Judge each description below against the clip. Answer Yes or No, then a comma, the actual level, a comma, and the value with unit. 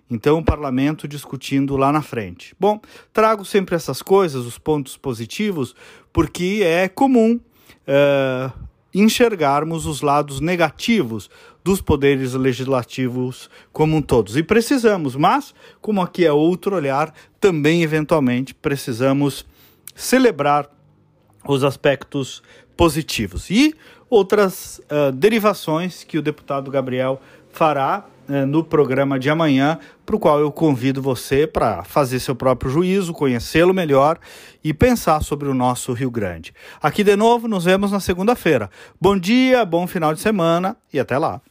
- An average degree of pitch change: No, wide, 5.8 semitones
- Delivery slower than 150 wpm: Yes, average, 135 wpm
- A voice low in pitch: No, medium, 150 Hz